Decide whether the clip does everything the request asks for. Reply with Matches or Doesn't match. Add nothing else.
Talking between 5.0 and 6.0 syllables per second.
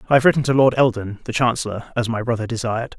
Doesn't match